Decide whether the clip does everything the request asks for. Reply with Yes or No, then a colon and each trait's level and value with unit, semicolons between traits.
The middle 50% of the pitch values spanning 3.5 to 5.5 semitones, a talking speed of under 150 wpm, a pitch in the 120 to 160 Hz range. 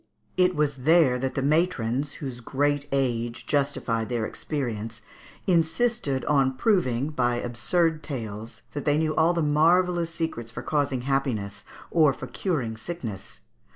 Yes: average, 4.9 semitones; average, 140 wpm; medium, 140 Hz